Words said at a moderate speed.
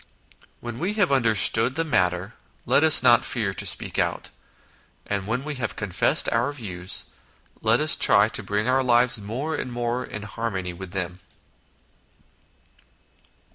Yes: average, 150 wpm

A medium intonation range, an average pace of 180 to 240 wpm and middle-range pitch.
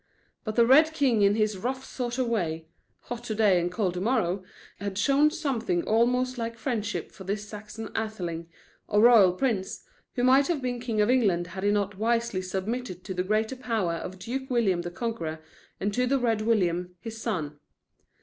No: average, 4.6 semitones; average, 190 wpm; high, 215 Hz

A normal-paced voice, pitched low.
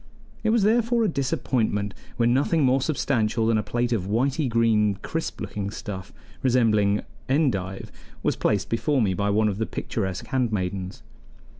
Yes: average, 155 wpm; low, 115 Hz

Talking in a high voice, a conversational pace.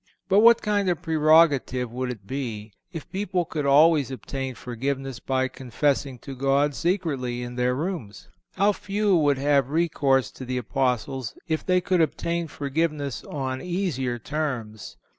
No: medium, 140 Hz; average, 150 wpm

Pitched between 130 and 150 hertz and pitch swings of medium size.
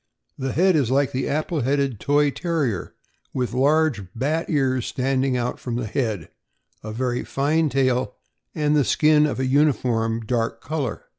Yes: low, 135 Hz; average, 3.4 semitones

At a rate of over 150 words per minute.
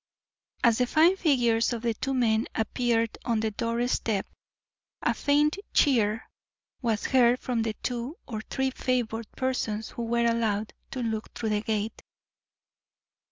No: average, 145 wpm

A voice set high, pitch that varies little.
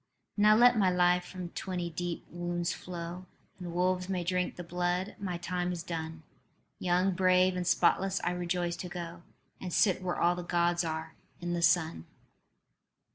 No: medium, 180 Hz; narrow, 1.0 semitones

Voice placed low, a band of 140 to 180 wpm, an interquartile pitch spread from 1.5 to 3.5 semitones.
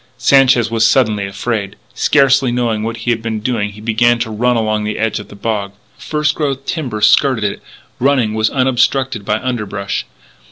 Yes: low, 115 Hz; average, 170 wpm; average, 3.2 semitones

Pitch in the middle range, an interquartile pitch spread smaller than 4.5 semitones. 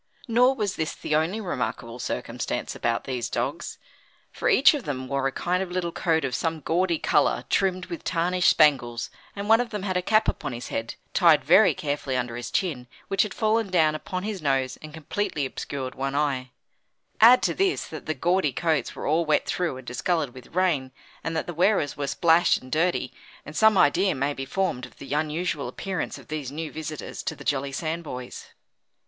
No: medium, 160 Hz; average, 5.2 semitones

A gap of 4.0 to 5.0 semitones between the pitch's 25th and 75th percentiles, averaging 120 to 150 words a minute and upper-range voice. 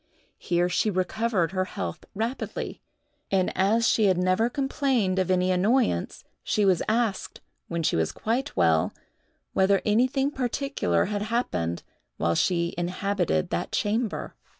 Yes: average, 4.6 semitones; slow, 135 wpm; high, 195 Hz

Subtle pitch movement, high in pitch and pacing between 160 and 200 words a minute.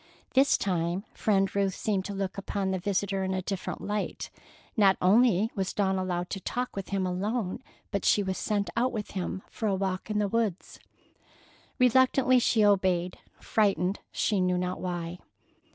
Yes: narrow, 2.3 semitones; high, 195 Hz; average, 170 wpm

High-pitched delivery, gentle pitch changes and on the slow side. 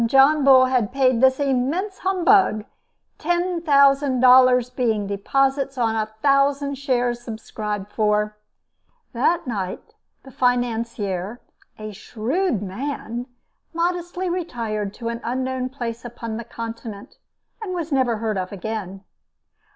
No: very high, 250 Hz; average, 4.1 semitones; slow, 115 wpm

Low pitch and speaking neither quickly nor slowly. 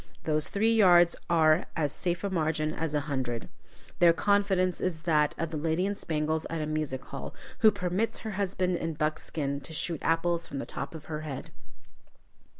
No: medium, 165 Hz; average, 185 wpm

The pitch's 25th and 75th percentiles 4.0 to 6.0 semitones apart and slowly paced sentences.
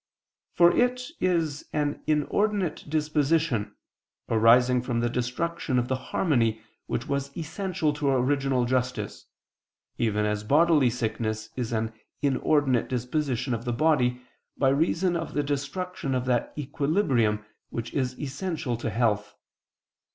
Yes: average, 4.4 semitones; slow, 130 wpm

